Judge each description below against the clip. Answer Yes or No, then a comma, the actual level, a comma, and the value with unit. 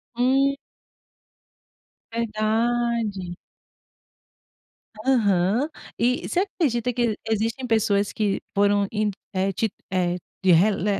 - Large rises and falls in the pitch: No, average, 3.2 semitones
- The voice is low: No, high, 220 Hz